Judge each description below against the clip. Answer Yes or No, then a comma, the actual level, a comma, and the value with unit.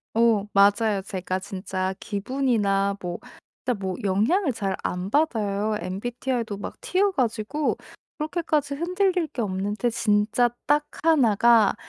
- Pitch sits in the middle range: No, high, 220 Hz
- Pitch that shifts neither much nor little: No, wide, 5.7 semitones